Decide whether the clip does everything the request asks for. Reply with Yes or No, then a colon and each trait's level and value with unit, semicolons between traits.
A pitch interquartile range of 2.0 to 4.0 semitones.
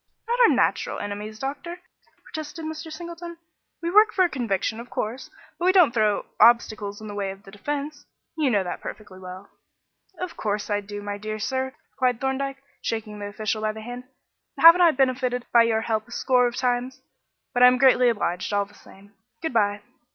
No: average, 5.0 semitones